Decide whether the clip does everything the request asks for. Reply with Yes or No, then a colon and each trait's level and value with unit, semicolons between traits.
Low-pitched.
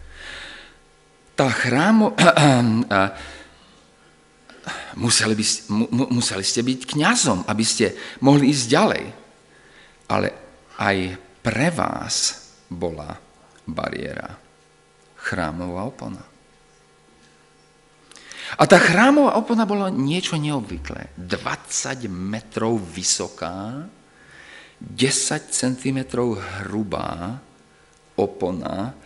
Yes: low, 115 Hz